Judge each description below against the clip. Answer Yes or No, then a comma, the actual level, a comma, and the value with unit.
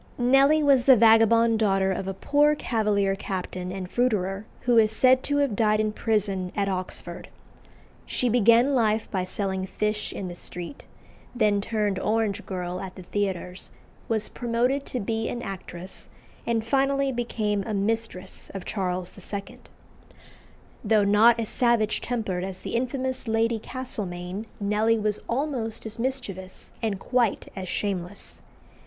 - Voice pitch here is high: Yes, high, 215 Hz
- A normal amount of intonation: Yes, average, 3.5 semitones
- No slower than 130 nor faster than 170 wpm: Yes, average, 150 wpm